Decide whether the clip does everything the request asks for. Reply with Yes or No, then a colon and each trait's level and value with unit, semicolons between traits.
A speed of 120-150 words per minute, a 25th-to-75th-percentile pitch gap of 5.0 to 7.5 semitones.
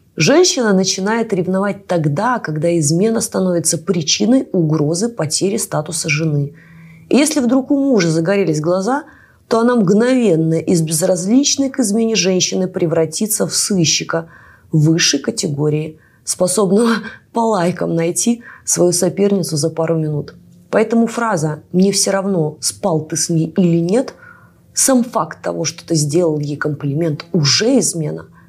Yes: average, 130 wpm; wide, 5.4 semitones